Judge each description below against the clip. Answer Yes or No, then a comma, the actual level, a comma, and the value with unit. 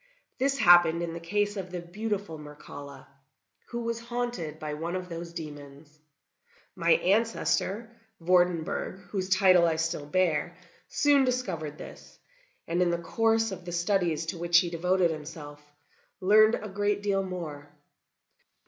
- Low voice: No, medium, 175 Hz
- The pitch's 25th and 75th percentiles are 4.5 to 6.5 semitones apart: No, average, 4.0 semitones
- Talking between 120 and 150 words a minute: Yes, average, 145 wpm